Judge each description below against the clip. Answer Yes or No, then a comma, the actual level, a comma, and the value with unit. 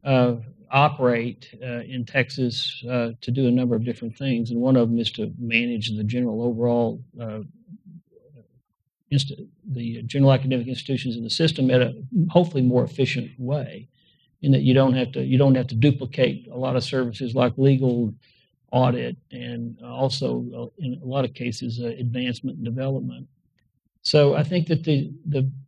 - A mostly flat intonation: Yes, narrow, 2.2 semitones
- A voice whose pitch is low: Yes, low, 125 Hz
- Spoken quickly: No, average, 170 wpm